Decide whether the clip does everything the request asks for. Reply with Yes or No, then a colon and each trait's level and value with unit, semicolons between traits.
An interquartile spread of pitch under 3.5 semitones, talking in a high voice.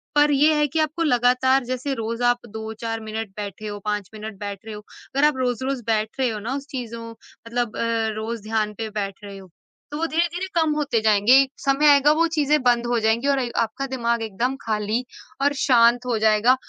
No: average, 3.9 semitones; high, 240 Hz